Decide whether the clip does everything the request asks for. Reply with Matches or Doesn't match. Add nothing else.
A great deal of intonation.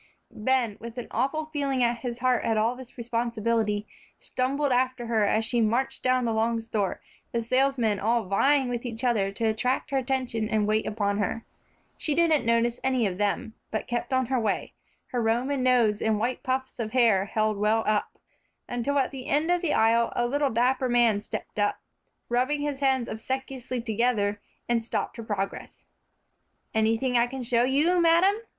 Doesn't match